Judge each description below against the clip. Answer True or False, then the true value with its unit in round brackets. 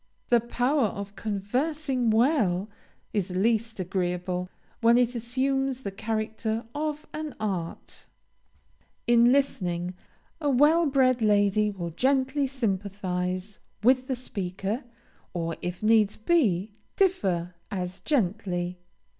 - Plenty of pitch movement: True (5.7 semitones)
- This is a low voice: False (220 Hz)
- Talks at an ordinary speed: False (115 wpm)